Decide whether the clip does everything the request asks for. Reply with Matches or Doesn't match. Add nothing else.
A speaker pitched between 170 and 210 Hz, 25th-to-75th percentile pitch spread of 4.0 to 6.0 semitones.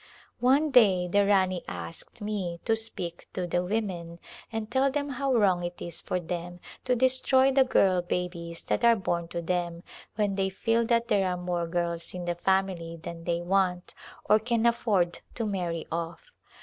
Matches